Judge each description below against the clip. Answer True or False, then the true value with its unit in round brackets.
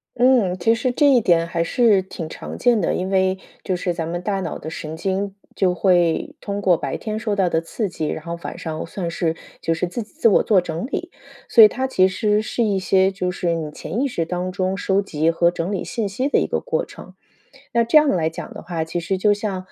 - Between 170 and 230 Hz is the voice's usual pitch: True (190 Hz)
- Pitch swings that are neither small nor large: True (3.9 semitones)